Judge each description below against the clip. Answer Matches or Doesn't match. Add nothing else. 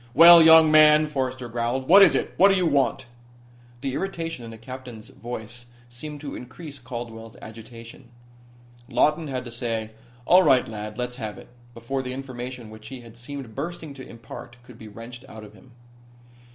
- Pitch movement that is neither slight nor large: Matches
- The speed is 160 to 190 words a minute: Matches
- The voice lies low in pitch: Matches